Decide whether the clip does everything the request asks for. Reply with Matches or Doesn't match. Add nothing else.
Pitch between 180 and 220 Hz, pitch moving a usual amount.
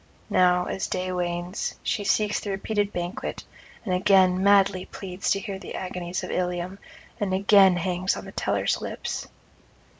Doesn't match